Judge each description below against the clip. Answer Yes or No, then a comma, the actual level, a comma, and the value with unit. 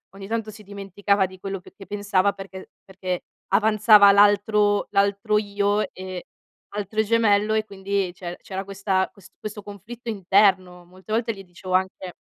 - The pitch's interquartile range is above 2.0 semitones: No, narrow, 1.7 semitones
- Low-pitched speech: No, high, 200 Hz